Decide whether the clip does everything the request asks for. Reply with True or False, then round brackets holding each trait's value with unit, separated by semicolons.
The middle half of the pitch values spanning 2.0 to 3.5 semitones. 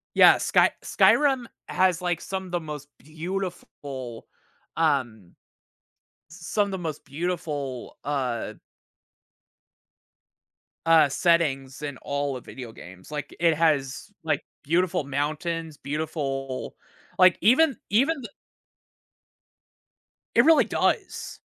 False (4.5 semitones)